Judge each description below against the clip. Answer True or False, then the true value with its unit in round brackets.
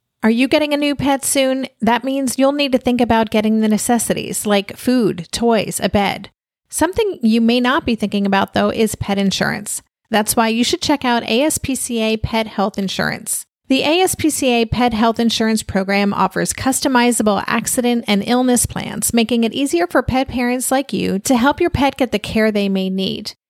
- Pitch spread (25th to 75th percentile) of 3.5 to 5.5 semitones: True (4.1 semitones)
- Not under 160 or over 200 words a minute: True (185 wpm)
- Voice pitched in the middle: False (235 Hz)